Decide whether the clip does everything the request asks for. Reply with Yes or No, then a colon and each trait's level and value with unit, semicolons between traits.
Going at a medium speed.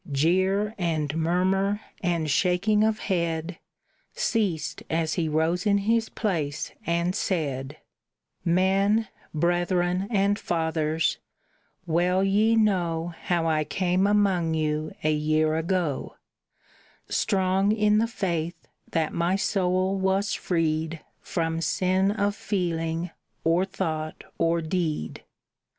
No: slow, 110 wpm